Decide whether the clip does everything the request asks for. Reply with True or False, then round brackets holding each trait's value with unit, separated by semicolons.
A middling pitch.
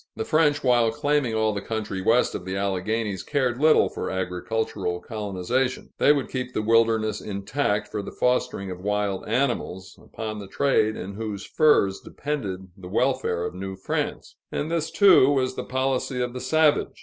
False (110 Hz)